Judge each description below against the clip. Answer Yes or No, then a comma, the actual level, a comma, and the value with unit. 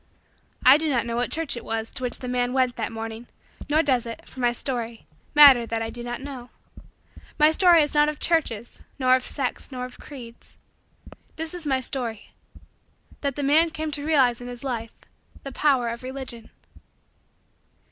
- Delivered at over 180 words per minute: Yes, average, 190 wpm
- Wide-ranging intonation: No, average, 3.4 semitones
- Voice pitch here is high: Yes, very high, 255 Hz